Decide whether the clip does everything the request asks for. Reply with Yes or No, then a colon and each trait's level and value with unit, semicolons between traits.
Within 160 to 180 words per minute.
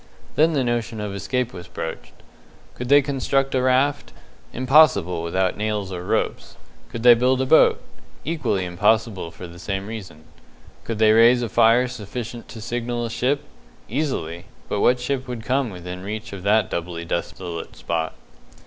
Yes: average, 165 wpm